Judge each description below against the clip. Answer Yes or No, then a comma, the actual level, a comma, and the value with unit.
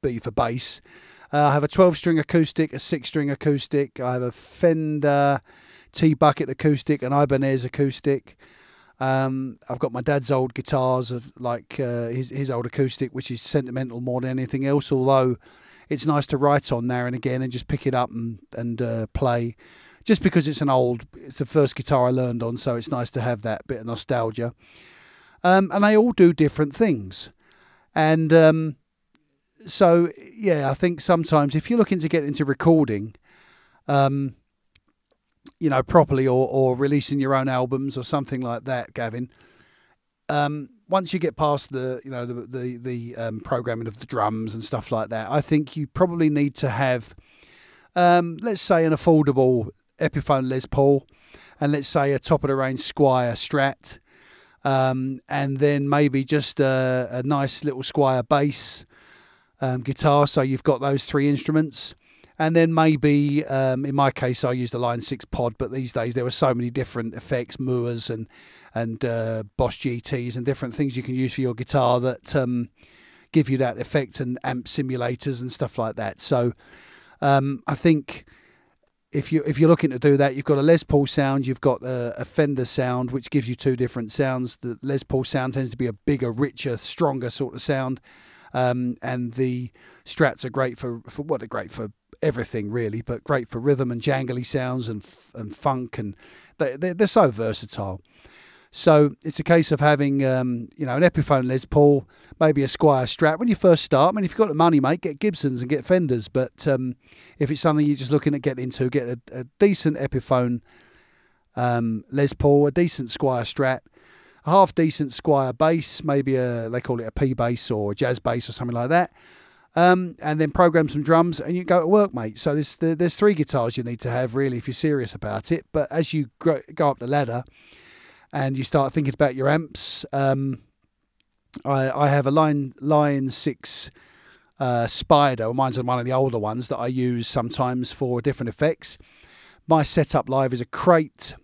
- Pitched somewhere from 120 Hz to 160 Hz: Yes, low, 135 Hz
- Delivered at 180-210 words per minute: Yes, average, 195 wpm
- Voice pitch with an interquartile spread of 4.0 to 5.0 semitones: No, average, 3.3 semitones